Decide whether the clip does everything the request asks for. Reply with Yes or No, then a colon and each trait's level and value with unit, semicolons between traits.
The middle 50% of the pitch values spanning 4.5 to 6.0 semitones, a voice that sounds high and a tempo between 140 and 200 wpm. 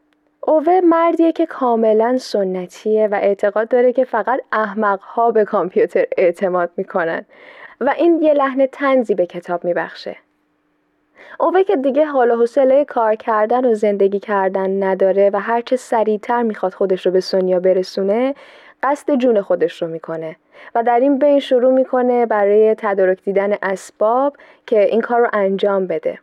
Yes: average, 5.1 semitones; high, 220 Hz; average, 150 wpm